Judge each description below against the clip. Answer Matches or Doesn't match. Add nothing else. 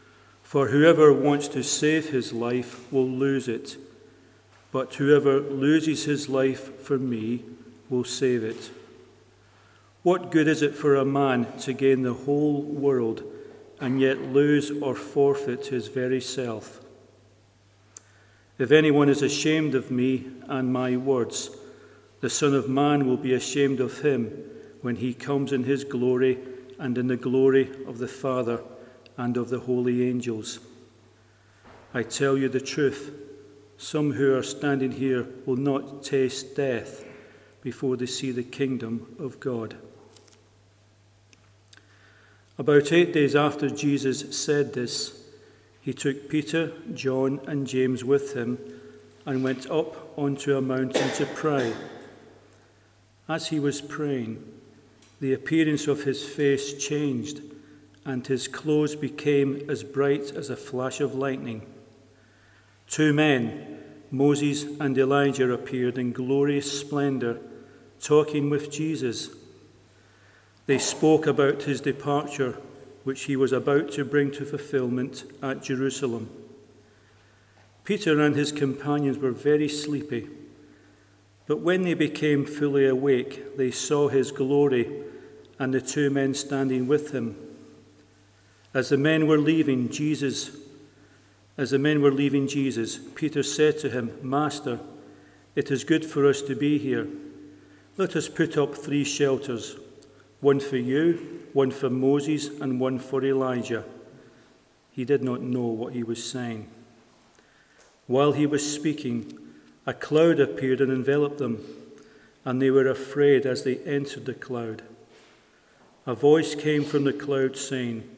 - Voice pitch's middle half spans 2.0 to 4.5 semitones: Matches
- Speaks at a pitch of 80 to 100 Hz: Doesn't match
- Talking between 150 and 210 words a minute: Doesn't match